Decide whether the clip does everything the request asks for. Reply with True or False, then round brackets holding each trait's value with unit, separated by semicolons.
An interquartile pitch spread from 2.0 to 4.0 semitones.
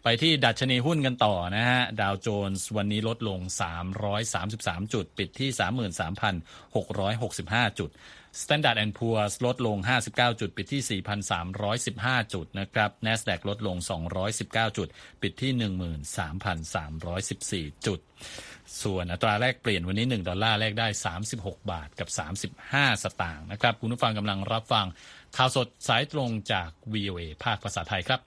True (3.4 semitones)